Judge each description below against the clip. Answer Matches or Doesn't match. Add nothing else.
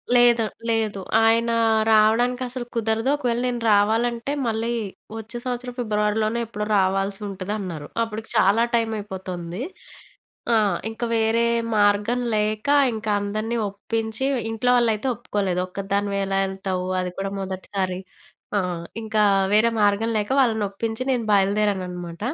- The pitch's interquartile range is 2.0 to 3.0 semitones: Matches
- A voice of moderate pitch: Doesn't match